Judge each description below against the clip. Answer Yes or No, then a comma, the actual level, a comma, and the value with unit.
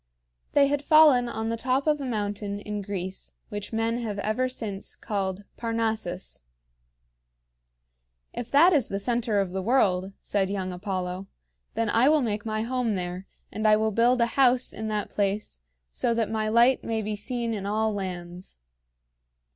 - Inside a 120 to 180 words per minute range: Yes, average, 170 wpm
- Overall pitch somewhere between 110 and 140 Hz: No, high, 215 Hz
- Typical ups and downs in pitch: Yes, average, 3.2 semitones